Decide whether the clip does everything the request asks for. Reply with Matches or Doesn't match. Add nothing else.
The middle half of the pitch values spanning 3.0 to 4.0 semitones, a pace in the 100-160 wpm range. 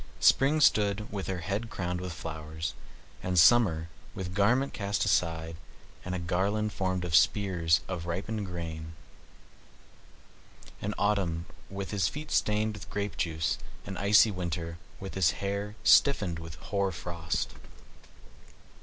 Matches